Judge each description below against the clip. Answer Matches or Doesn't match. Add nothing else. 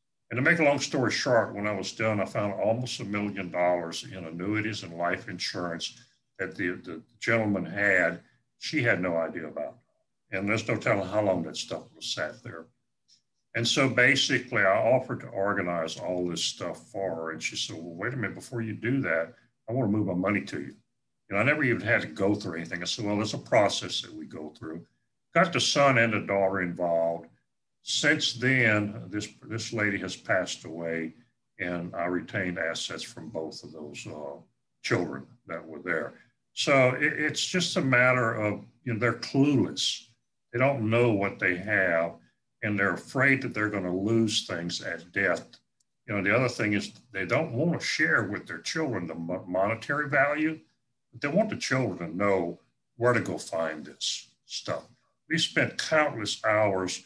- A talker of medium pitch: Doesn't match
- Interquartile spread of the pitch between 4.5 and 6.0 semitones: Matches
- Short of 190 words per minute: Doesn't match